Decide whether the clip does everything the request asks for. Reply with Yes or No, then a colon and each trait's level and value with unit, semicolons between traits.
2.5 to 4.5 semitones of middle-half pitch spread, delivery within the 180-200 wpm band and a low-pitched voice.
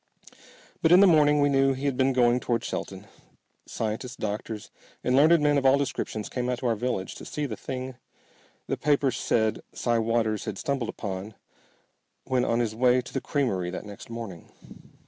Yes: average, 3.7 semitones; average, 185 wpm; low, 125 Hz